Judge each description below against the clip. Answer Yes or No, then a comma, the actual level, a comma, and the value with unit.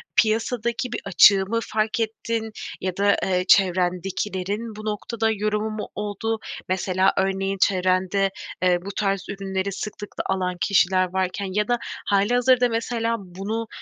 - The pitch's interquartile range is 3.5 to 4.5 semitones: No, average, 2.8 semitones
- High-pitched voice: Yes, high, 200 Hz